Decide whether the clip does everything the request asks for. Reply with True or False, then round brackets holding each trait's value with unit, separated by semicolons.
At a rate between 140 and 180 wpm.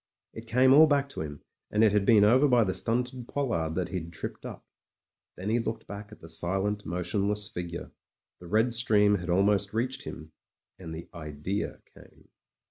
False (195 wpm)